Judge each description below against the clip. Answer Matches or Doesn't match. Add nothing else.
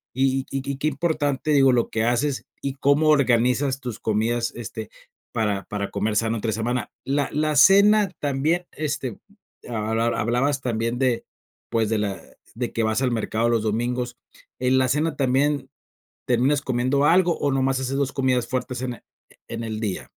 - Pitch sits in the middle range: Doesn't match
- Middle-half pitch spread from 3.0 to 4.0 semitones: Matches